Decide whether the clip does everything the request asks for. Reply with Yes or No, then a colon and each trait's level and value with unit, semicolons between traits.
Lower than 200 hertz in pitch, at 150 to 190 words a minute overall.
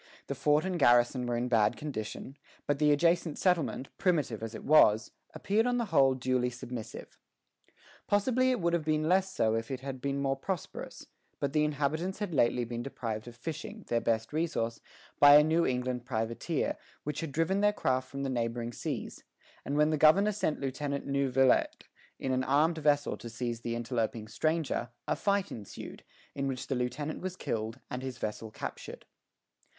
Yes: low, 135 Hz; average, 180 wpm